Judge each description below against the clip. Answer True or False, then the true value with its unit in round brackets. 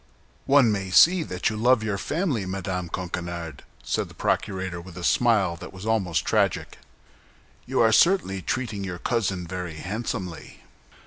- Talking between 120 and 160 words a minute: True (150 wpm)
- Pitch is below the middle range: True (95 Hz)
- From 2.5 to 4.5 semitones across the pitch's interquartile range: True (3.9 semitones)